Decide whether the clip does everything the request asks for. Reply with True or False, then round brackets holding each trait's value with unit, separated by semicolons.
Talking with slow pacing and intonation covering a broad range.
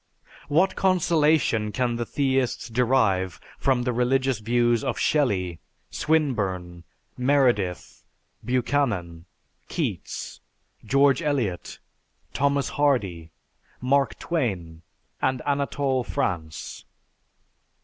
True (85 wpm; 6.0 semitones)